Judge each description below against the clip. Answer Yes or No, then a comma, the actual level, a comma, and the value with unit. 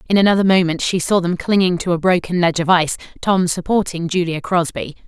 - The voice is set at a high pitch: No, medium, 175 Hz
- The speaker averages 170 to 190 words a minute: No, average, 200 wpm